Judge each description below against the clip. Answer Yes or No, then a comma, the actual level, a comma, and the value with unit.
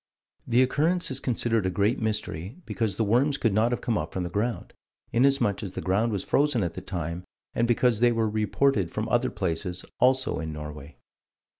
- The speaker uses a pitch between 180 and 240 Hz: No, low, 110 Hz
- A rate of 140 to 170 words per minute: No, average, 195 wpm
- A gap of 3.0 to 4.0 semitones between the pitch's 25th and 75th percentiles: No, average, 4.9 semitones